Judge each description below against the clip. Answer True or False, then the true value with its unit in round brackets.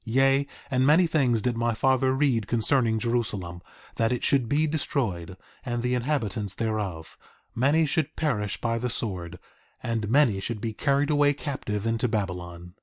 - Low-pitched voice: True (120 Hz)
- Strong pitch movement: False (4.6 semitones)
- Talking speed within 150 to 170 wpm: True (155 wpm)